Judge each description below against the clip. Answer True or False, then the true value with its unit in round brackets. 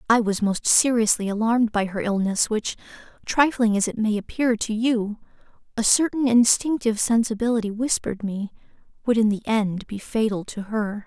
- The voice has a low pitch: False (220 Hz)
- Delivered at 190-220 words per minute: False (165 wpm)